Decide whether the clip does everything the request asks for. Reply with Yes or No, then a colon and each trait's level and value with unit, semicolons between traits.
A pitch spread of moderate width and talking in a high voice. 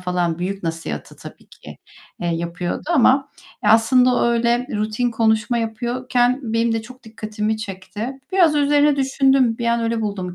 Yes: average, 3.3 semitones; high, 230 Hz